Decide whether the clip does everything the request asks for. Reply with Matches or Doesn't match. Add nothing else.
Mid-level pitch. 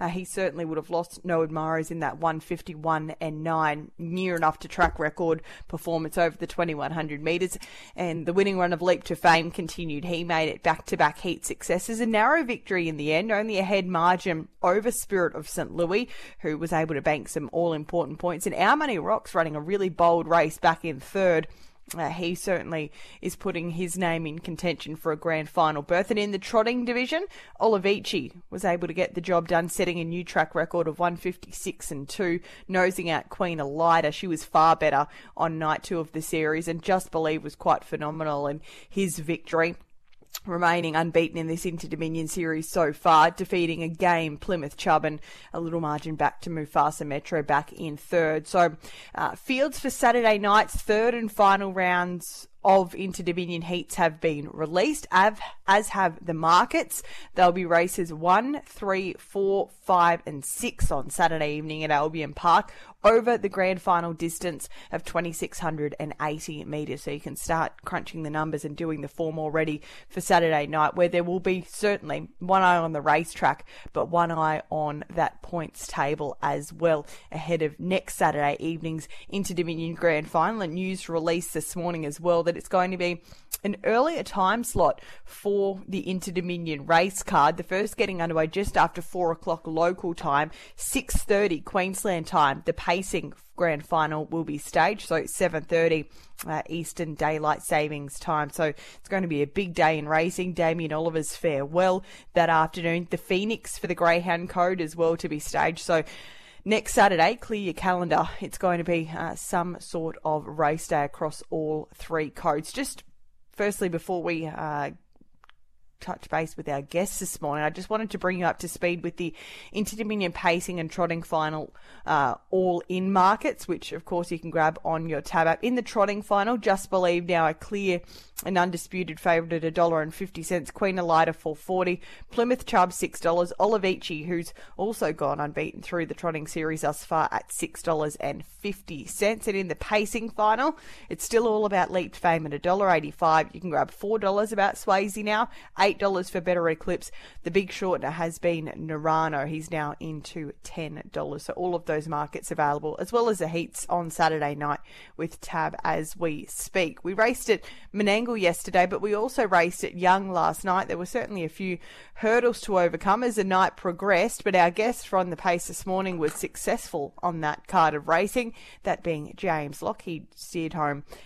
Matches